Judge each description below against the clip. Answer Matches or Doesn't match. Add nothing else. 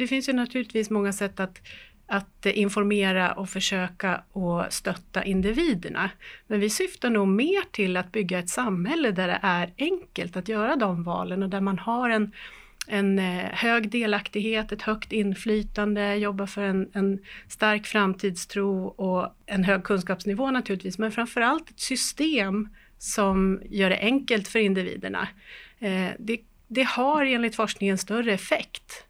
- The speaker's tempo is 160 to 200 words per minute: Doesn't match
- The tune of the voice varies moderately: Matches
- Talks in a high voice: Matches